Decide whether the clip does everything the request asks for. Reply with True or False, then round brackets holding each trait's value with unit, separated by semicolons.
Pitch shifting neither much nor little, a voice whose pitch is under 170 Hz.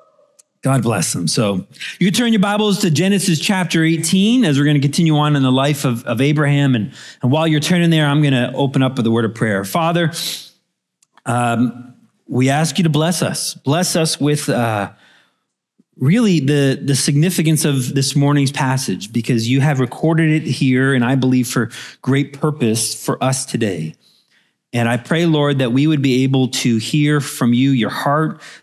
True (4.0 semitones; 140 Hz)